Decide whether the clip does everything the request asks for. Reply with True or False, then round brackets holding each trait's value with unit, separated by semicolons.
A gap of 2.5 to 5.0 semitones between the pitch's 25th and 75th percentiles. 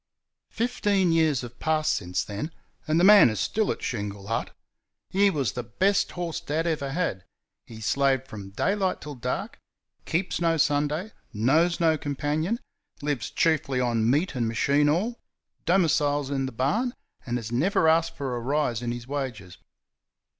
False (5.6 semitones)